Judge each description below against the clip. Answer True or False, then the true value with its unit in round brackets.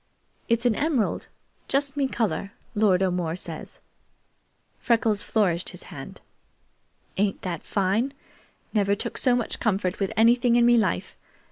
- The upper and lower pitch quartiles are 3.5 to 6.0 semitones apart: True (3.8 semitones)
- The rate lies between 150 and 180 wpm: False (135 wpm)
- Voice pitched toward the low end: False (215 Hz)